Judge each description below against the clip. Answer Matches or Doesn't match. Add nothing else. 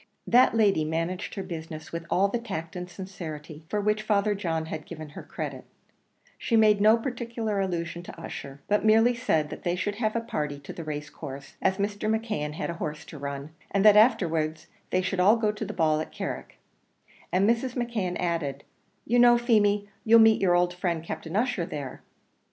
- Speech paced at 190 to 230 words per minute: Matches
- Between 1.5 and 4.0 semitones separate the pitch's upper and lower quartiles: Doesn't match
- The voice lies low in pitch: Doesn't match